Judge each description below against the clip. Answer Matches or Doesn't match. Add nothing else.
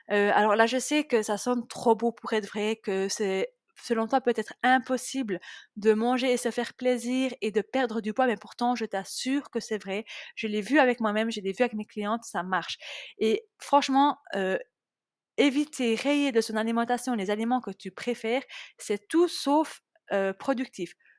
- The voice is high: Matches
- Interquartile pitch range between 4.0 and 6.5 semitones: Doesn't match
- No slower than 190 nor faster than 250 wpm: Matches